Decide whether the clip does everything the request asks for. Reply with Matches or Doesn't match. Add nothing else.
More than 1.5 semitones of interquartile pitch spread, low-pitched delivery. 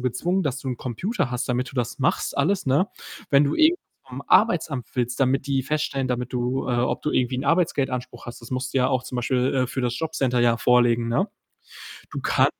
Matches